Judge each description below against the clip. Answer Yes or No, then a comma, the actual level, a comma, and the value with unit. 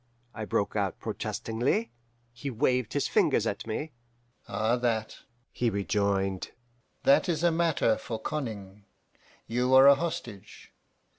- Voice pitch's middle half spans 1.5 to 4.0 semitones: No, average, 5.1 semitones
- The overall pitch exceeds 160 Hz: No, low, 120 Hz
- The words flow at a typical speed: No, slow, 130 wpm